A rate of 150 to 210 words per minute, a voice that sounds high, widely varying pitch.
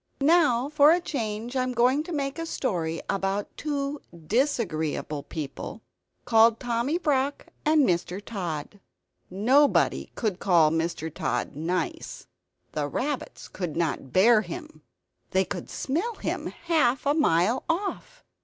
No: slow, 135 wpm; high, 235 Hz; wide, 8.4 semitones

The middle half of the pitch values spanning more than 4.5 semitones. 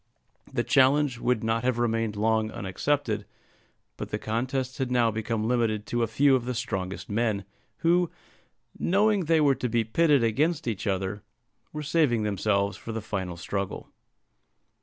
No: average, 4.2 semitones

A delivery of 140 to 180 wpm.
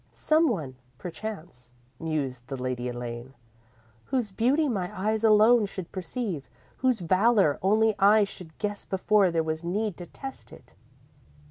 Yes: average, 145 wpm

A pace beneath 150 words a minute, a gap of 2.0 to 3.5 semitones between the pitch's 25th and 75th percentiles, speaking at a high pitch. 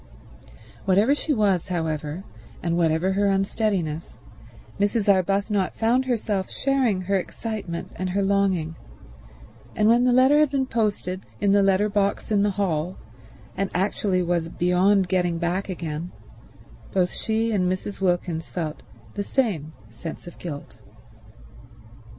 Yes: slow, 135 wpm; average, 3.1 semitones; high, 195 Hz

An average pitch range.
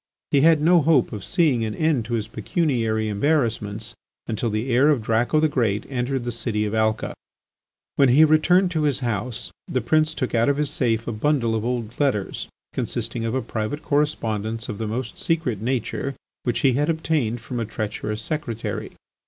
Yes: average, 4.9 semitones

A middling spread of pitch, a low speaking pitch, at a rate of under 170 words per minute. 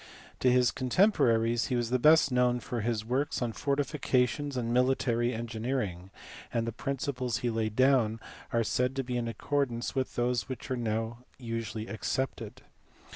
No: narrow, 2.1 semitones; low, 120 Hz; average, 155 wpm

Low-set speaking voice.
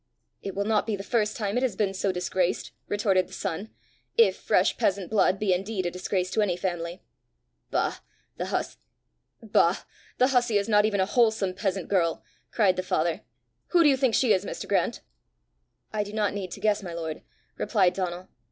No: high, 195 Hz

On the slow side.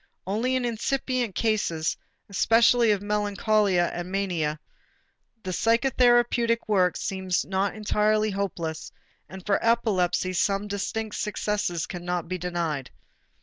Yes: slow, 110 wpm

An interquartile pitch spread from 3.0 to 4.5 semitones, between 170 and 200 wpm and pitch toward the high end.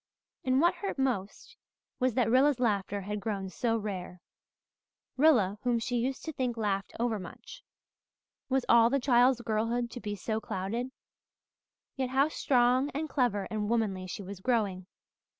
No: average, 4.0 semitones; average, 155 wpm; high, 235 Hz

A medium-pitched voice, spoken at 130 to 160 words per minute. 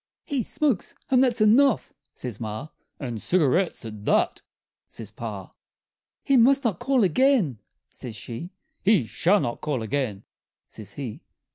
Yes: medium, 150 Hz; average, 140 wpm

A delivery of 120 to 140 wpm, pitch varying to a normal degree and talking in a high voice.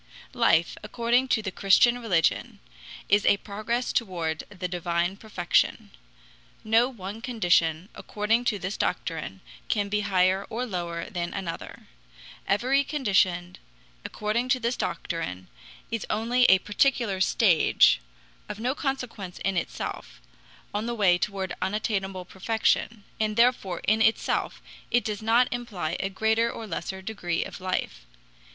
Yes: slow, 135 wpm; average, 4.0 semitones; high, 205 Hz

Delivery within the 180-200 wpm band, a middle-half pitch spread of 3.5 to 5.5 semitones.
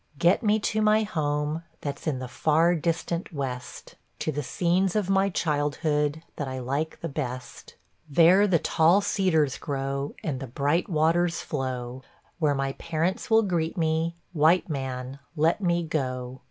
No: average, 155 wpm; average, 3.9 semitones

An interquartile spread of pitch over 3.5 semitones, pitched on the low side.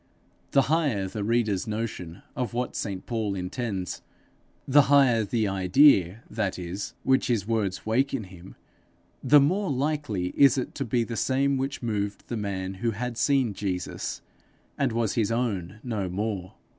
Yes: average, 4.8 semitones; low, 110 Hz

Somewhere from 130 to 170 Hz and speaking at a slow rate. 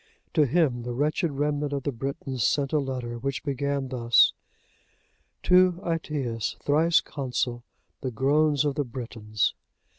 Yes: medium, 140 Hz; slow, 130 wpm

